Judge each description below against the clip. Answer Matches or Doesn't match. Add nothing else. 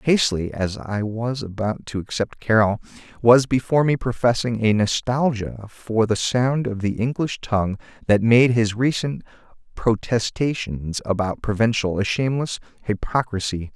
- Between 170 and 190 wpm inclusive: Doesn't match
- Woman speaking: Doesn't match